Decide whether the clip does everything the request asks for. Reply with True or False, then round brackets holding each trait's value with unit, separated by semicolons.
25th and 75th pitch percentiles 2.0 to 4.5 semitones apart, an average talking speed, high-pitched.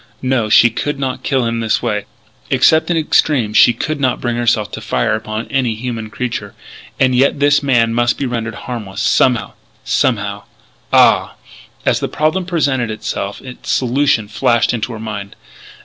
False (3.3 semitones; 165 wpm; 120 Hz)